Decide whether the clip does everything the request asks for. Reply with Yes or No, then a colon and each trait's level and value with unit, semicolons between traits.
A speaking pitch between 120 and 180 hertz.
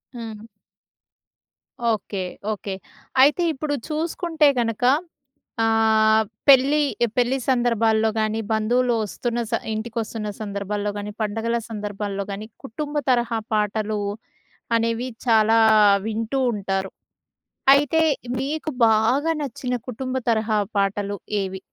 No: high, 225 Hz